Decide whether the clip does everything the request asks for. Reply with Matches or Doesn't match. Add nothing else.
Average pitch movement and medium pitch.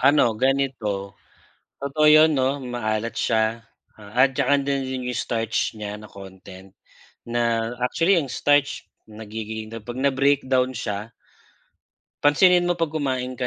Doesn't match